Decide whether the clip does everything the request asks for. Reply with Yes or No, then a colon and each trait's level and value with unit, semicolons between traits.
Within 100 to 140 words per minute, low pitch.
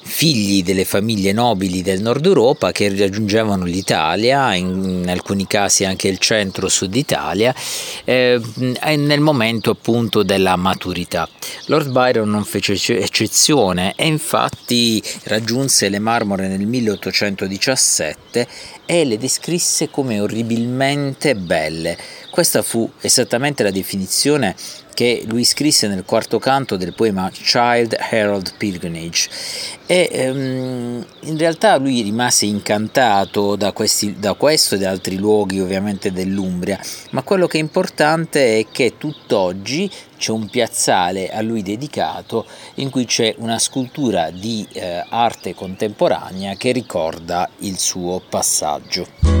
Yes: average, 120 wpm; low, 110 Hz